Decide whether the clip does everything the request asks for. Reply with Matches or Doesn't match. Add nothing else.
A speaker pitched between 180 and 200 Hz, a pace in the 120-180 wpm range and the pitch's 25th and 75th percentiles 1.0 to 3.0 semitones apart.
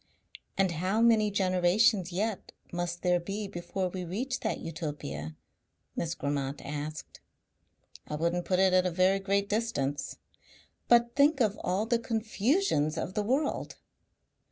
Doesn't match